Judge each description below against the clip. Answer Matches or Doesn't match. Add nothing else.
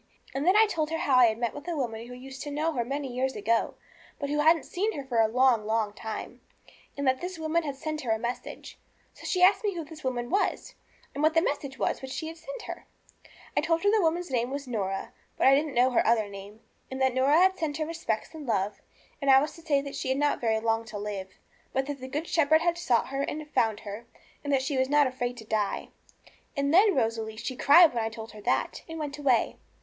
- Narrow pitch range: Doesn't match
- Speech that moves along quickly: Matches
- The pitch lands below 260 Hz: Doesn't match